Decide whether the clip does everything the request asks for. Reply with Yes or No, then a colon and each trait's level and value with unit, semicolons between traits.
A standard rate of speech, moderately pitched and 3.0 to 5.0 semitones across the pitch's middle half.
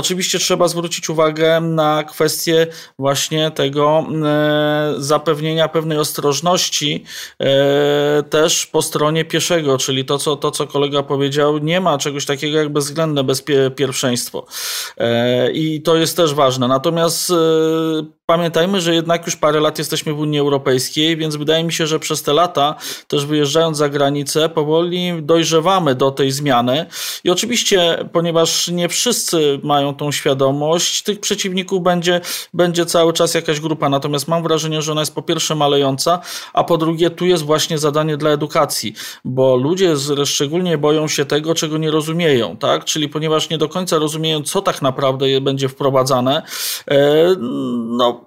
No: average, 145 wpm; medium, 155 Hz; narrow, 2.5 semitones